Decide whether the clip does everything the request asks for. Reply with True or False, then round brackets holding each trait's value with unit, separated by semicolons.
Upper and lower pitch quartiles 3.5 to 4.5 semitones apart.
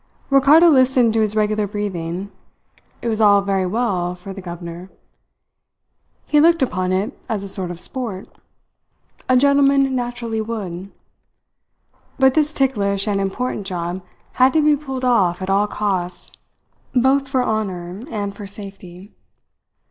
False (5.3 semitones)